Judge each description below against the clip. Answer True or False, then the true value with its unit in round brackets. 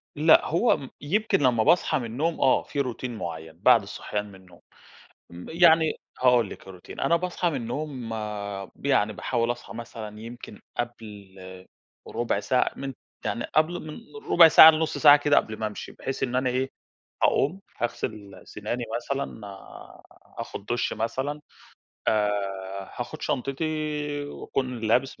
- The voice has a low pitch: True (125 Hz)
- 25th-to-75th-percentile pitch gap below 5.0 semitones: False (5.4 semitones)